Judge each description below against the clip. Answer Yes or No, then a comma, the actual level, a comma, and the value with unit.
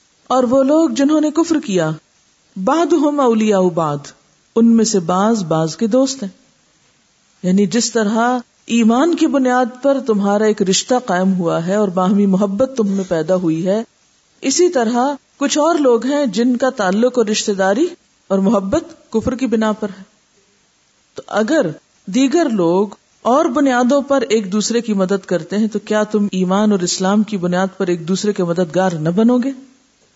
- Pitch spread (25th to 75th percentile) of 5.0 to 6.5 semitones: Yes, average, 5.3 semitones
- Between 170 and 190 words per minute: Yes, average, 175 wpm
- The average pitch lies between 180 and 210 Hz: No, high, 220 Hz